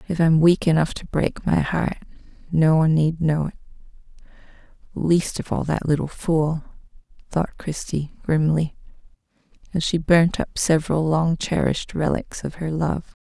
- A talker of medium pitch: Yes, medium, 160 Hz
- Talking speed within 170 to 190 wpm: No, average, 145 wpm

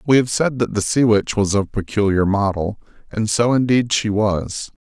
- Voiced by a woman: No, male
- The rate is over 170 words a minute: Yes, average, 200 wpm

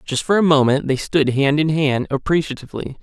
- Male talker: Yes, male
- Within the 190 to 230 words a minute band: Yes, average, 200 wpm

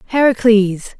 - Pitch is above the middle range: Yes, high, 225 Hz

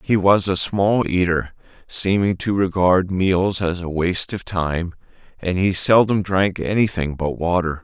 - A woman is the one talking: No, male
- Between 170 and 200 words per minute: No, average, 160 wpm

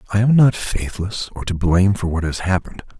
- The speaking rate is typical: No, fast, 220 wpm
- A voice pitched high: No, very low, 95 Hz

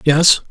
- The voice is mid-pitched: Yes, medium, 160 Hz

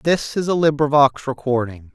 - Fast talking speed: No, average, 155 wpm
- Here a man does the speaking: Yes, male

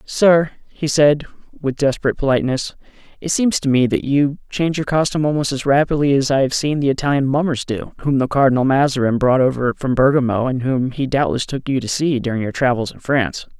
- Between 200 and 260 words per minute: Yes, fast, 205 wpm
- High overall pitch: No, low, 135 Hz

